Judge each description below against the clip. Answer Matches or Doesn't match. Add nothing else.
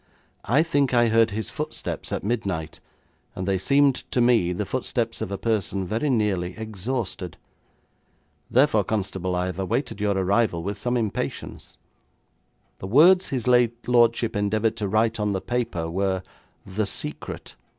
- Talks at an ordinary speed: Matches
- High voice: Doesn't match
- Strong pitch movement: Doesn't match